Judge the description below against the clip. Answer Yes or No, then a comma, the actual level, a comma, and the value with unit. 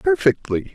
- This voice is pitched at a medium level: No, low, 105 Hz